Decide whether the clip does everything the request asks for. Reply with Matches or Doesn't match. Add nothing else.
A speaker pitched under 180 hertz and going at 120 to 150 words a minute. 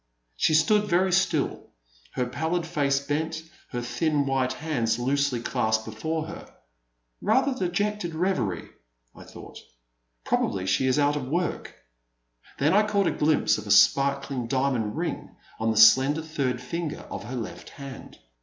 Doesn't match